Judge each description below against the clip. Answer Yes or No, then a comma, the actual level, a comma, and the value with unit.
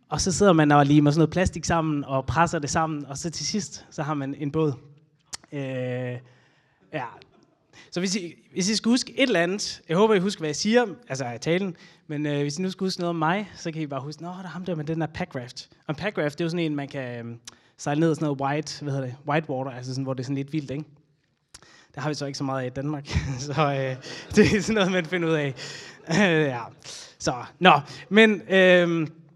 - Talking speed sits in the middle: No, fast, 260 wpm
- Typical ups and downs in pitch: Yes, average, 3.6 semitones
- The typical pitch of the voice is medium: Yes, medium, 155 Hz